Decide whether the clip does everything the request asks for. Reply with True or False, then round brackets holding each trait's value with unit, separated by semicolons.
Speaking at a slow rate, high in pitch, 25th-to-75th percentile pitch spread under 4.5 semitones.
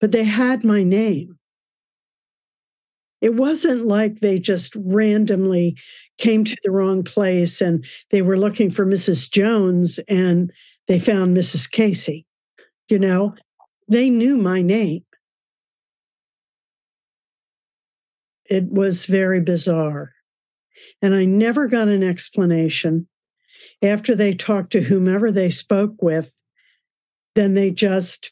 True (115 wpm; 195 Hz; 2.9 semitones)